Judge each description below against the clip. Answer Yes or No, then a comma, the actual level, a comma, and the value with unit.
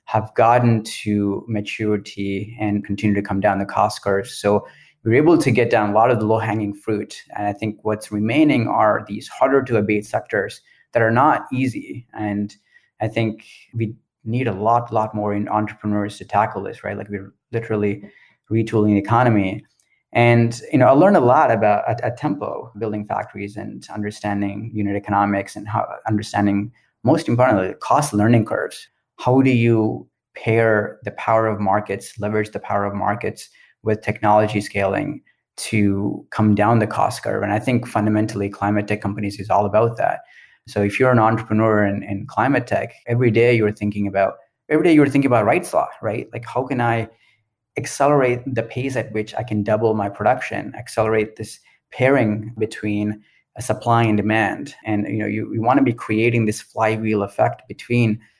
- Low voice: Yes, low, 110 Hz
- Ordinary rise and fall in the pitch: No, narrow, 1.9 semitones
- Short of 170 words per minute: No, average, 180 wpm